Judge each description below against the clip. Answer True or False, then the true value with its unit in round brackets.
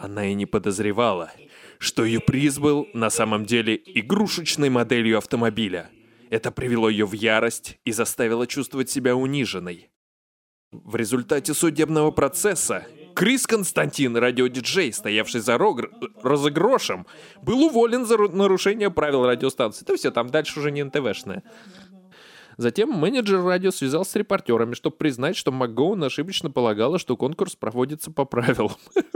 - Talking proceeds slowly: False (135 wpm)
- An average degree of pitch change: False (7.5 semitones)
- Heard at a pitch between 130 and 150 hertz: True (135 Hz)